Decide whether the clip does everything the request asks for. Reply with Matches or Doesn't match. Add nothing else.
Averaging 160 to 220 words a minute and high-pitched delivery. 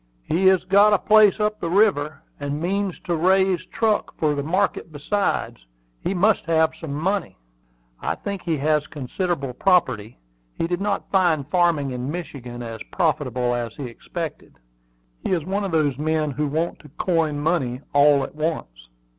Doesn't match